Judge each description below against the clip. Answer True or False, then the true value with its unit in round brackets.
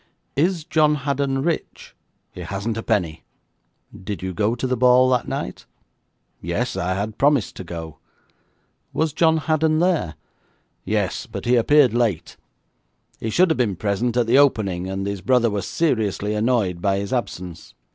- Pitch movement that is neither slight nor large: False (6.2 semitones)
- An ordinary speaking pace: True (160 wpm)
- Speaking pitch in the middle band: False (115 Hz)